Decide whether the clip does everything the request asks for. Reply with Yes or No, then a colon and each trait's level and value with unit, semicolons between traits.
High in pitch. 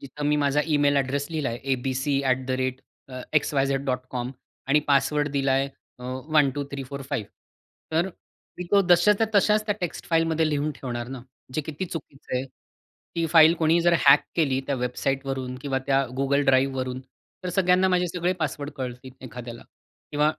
No: medium, 140 Hz